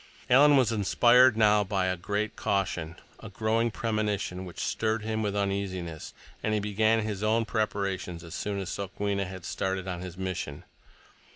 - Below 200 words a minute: Yes, average, 165 wpm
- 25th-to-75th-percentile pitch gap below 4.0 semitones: Yes, average, 2.8 semitones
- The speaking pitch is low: Yes, low, 100 Hz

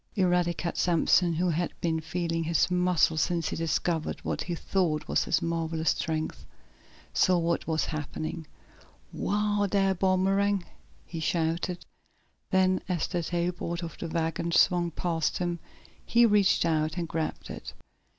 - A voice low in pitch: No, medium, 170 Hz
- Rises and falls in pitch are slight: Yes, narrow, 2.0 semitones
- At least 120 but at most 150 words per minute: Yes, average, 140 wpm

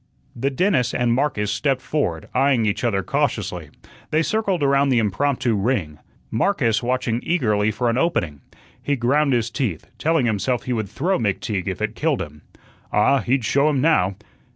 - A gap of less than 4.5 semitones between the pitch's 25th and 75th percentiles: No, average, 5.0 semitones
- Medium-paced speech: Yes, average, 170 wpm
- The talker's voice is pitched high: No, low, 120 Hz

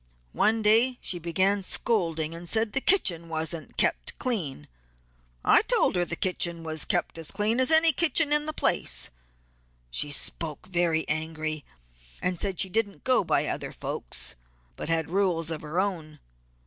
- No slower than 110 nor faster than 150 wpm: No, average, 165 wpm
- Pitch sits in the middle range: Yes, medium, 175 Hz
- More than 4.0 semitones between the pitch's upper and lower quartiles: Yes, average, 5.2 semitones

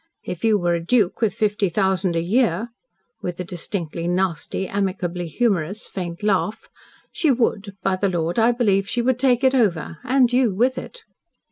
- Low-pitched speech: No, high, 195 Hz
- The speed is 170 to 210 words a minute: Yes, average, 175 wpm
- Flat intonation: No, average, 4.9 semitones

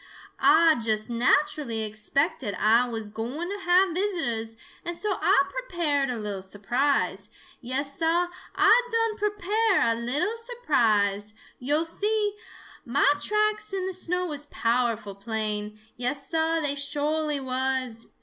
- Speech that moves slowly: Yes, slow, 130 wpm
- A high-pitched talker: Yes, very high, 285 Hz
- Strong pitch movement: Yes, wide, 7.9 semitones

